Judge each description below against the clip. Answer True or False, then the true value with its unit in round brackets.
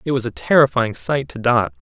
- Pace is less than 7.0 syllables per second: True (5.4 syllables/s)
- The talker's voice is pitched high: False (125 Hz)